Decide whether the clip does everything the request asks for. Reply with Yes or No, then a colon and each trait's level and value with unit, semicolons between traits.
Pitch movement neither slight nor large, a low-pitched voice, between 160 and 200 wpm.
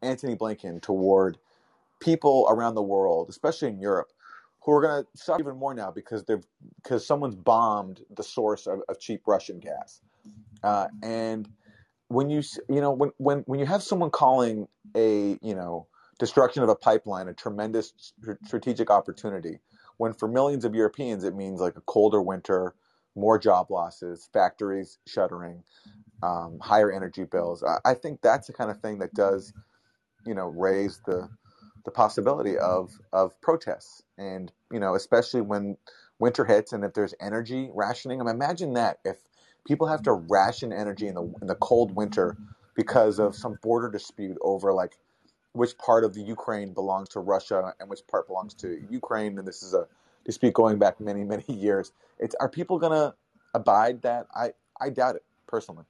Yes: average, 4.0 semitones; low, 105 Hz; average, 175 wpm